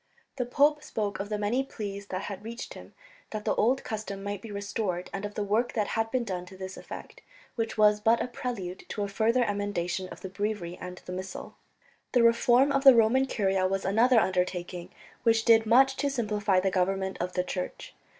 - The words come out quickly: Yes, fast, 210 wpm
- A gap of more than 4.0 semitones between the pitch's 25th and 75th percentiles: No, average, 3.4 semitones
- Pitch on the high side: Yes, high, 210 Hz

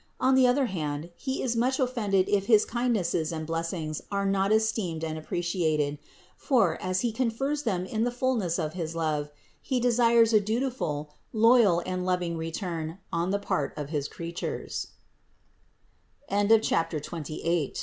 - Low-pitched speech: No, high, 195 Hz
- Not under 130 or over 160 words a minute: Yes, average, 140 wpm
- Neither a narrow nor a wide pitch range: No, wide, 6.3 semitones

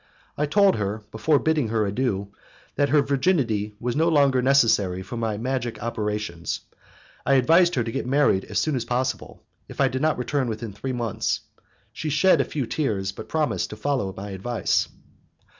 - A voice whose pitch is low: Yes, low, 125 Hz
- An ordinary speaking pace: Yes, average, 180 wpm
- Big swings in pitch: No, average, 5.0 semitones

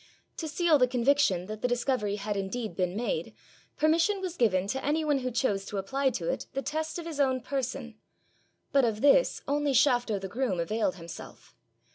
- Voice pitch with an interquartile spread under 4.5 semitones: No, wide, 5.6 semitones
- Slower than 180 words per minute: No, average, 190 wpm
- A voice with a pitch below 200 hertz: No, very high, 250 Hz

